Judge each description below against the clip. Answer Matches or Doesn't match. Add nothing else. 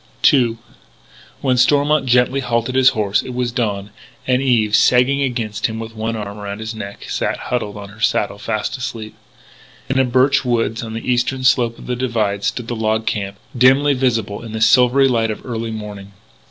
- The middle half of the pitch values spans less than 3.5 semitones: Matches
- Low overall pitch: Matches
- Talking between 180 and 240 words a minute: Matches